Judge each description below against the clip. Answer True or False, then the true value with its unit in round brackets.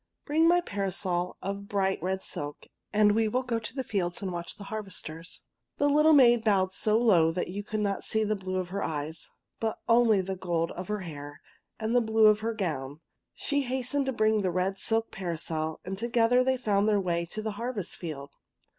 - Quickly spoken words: True (210 wpm)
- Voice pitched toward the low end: False (205 Hz)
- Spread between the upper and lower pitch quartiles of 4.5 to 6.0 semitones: False (4.1 semitones)